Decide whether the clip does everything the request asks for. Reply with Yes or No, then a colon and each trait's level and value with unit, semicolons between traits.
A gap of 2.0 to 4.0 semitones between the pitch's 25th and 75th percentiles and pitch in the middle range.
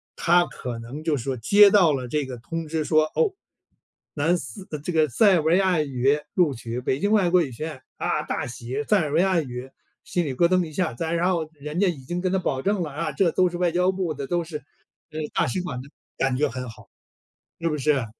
No: average, 4.8 semitones; medium, 155 Hz